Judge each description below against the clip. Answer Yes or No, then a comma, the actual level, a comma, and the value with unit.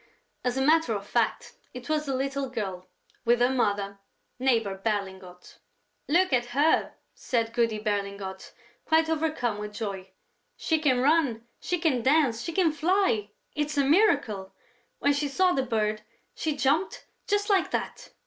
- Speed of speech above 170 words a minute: No, average, 155 wpm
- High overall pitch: Yes, very high, 255 Hz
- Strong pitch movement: Yes, wide, 6.5 semitones